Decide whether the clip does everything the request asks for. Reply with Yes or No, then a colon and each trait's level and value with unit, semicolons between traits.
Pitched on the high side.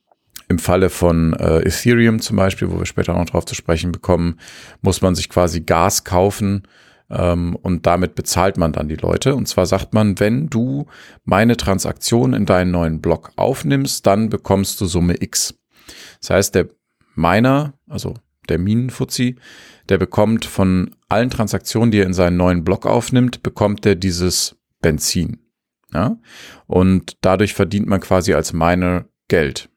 No: very low, 95 Hz